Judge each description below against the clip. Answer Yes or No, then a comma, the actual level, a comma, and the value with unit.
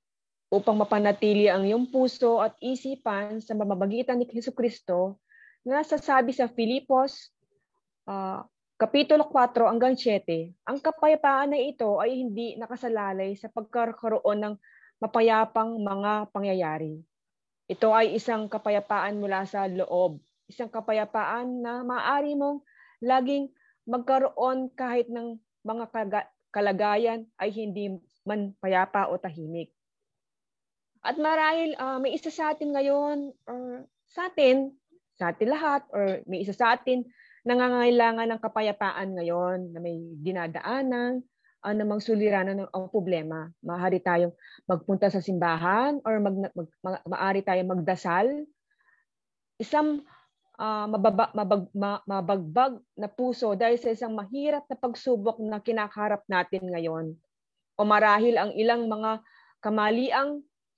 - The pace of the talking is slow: No, average, 120 wpm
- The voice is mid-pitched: No, high, 220 Hz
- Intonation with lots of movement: No, average, 4.4 semitones